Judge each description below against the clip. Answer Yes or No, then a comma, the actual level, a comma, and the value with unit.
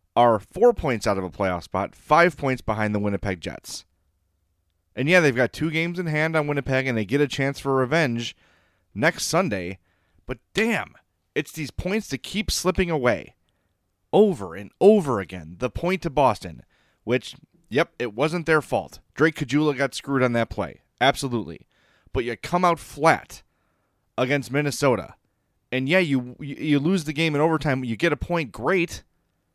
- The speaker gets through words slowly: No, average, 175 wpm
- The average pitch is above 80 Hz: Yes, low, 135 Hz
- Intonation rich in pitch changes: Yes, wide, 6.6 semitones